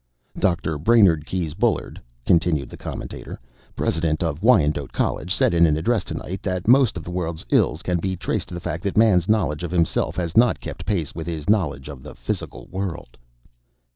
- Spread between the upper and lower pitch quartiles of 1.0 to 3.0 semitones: No, average, 3.4 semitones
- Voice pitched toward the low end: Yes, very low, 85 Hz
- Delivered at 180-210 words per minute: Yes, average, 190 wpm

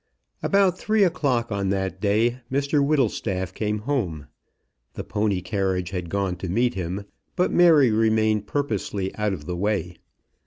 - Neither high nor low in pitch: No, low, 105 Hz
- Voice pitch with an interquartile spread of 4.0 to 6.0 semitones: Yes, wide, 5.5 semitones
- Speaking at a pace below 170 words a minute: Yes, average, 150 wpm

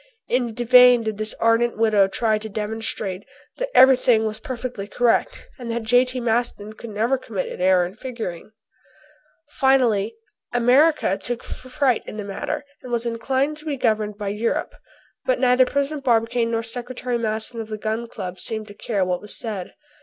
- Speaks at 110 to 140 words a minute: No, average, 170 wpm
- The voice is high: Yes, high, 230 Hz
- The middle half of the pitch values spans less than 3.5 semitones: Yes, average, 2.7 semitones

